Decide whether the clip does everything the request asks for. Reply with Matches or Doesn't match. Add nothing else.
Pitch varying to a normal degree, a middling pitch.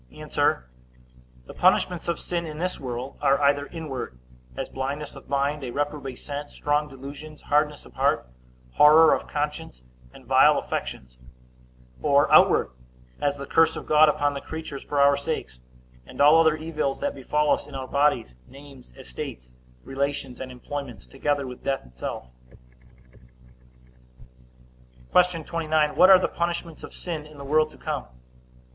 Doesn't match